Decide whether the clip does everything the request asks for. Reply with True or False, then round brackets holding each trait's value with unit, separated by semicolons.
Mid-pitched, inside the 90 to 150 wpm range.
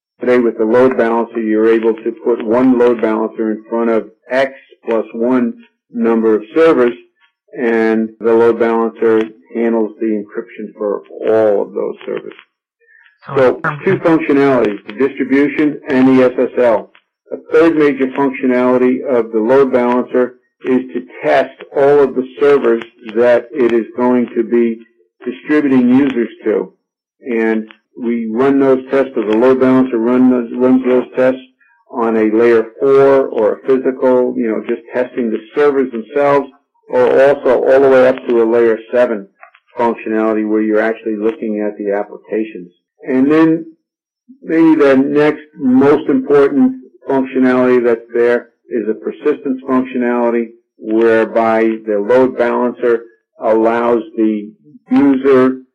False (125 Hz; 140 wpm)